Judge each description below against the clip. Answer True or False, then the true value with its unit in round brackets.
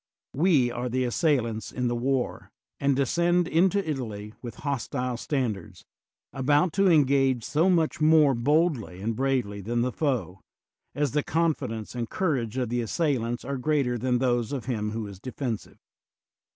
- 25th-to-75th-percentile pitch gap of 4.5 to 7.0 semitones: False (4.1 semitones)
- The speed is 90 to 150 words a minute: False (165 wpm)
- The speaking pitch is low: True (130 Hz)